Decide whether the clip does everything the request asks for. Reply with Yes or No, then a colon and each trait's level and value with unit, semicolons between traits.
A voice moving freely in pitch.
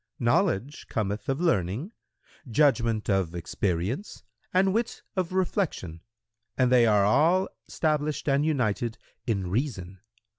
Yes: wide, 7.8 semitones